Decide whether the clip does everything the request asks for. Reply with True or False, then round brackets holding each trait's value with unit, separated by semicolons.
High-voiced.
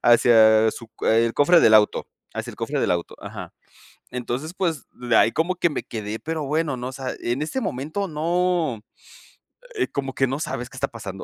False (130 Hz)